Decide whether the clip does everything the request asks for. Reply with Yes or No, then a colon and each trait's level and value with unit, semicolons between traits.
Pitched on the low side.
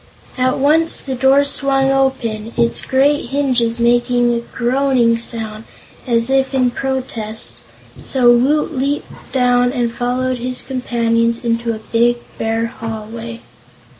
No: high, 245 Hz